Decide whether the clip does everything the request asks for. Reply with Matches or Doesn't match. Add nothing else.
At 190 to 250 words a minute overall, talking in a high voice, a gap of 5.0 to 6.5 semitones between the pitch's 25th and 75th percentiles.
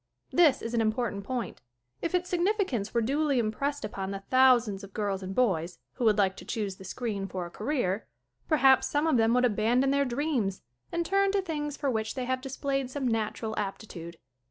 Matches